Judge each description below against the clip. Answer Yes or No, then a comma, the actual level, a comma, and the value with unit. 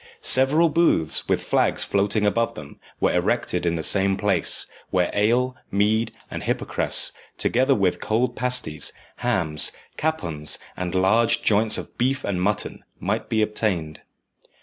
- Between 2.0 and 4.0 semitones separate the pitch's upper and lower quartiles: No, average, 5.0 semitones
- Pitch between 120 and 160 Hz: No, low, 105 Hz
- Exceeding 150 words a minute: No, average, 140 wpm